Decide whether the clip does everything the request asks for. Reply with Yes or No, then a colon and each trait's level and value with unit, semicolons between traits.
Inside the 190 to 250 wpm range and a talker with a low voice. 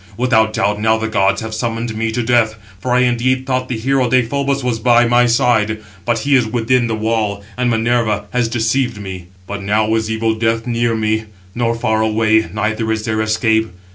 Yes: average, 200 wpm; low, 115 Hz